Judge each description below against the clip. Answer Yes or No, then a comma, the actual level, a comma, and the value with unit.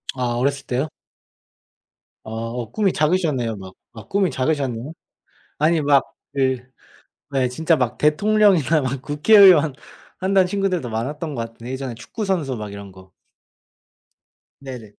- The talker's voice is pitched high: No, medium, 140 Hz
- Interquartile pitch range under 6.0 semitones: Yes, average, 5.3 semitones